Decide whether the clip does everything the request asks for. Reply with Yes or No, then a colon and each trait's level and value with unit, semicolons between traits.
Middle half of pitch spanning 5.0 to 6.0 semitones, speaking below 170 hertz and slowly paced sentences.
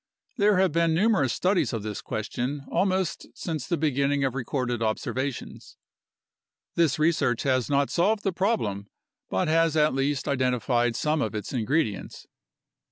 No: wide, 5.5 semitones; medium, 140 Hz; average, 145 wpm